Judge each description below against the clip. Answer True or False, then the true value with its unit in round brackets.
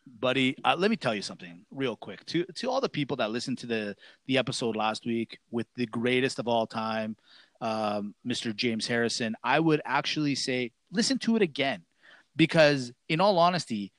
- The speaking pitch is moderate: False (125 Hz)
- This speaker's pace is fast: False (190 wpm)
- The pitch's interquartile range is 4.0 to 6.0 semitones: True (5.1 semitones)